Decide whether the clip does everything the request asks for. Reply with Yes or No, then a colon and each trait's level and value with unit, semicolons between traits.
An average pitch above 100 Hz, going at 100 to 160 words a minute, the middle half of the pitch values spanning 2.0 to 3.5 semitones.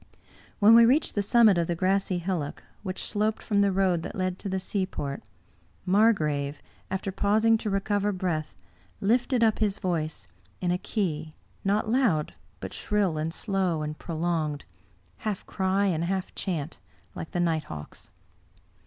No: high, 190 Hz; average, 155 wpm; average, 3.9 semitones